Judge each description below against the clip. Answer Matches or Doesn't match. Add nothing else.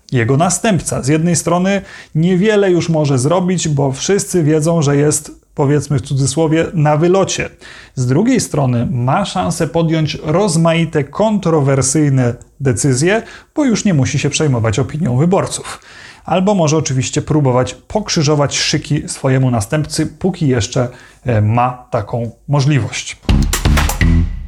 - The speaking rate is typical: Matches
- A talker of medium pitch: Matches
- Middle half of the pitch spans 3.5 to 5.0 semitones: Matches